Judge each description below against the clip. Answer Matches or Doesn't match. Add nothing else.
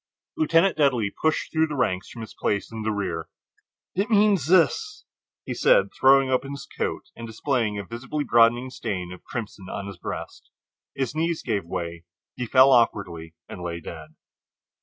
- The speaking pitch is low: Matches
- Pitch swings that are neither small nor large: Doesn't match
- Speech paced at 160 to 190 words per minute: Matches